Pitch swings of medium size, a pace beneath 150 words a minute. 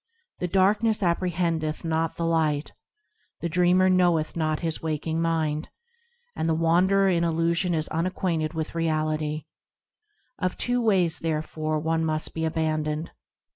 No: narrow, 2.2 semitones; slow, 135 wpm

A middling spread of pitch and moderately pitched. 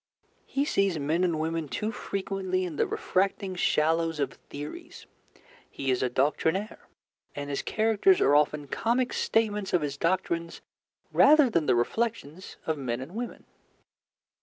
No: wide, 6.0 semitones; medium, 170 Hz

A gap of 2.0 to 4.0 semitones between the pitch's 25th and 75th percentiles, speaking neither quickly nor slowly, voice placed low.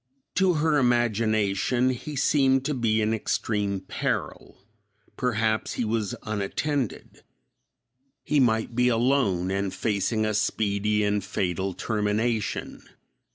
No: average, 3.3 semitones; slow, 110 wpm; low, 110 Hz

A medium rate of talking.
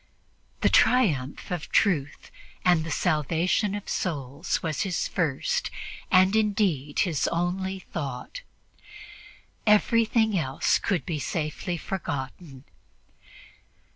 No: slow, 100 wpm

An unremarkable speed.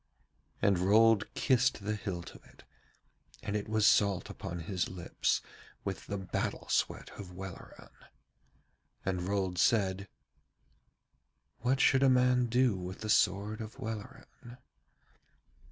No: slow, 125 wpm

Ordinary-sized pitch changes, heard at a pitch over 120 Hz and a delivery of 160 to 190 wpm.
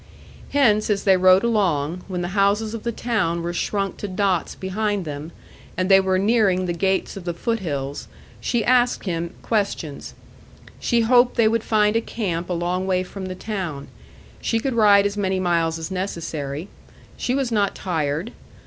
Yes: average, 3.8 semitones; high, 190 Hz; average, 180 wpm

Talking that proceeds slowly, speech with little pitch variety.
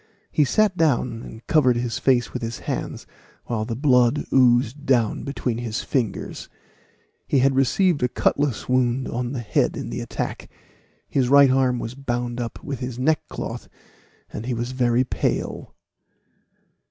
No: average, 155 wpm; narrow, 2.3 semitones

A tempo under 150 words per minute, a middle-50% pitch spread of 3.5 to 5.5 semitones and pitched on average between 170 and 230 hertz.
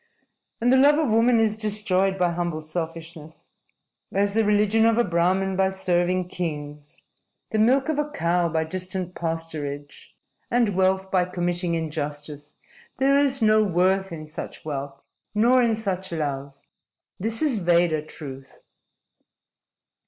Yes: average, 140 wpm; average, 5.0 semitones; medium, 185 Hz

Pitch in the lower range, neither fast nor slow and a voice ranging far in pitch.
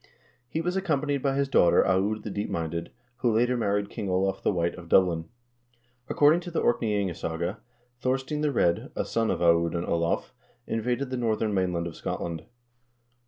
Yes: low, 105 Hz; average, 190 wpm; wide, 6.8 semitones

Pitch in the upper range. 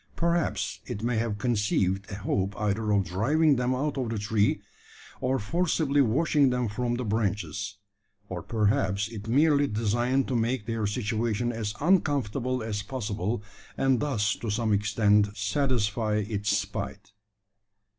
No: low, 110 Hz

